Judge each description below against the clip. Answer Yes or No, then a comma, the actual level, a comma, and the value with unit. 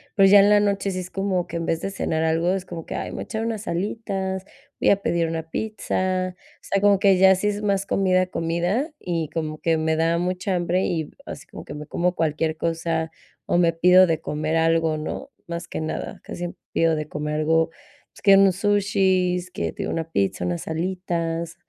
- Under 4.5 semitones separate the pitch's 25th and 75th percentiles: Yes, average, 2.9 semitones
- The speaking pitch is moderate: Yes, medium, 175 Hz